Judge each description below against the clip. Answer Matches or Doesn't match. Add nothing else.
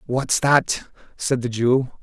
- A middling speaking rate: Matches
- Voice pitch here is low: Matches